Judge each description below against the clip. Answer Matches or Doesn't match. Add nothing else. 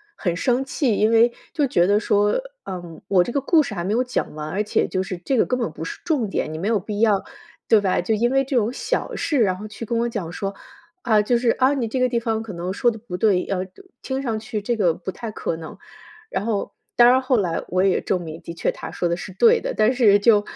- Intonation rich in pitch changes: Doesn't match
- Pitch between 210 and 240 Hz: Matches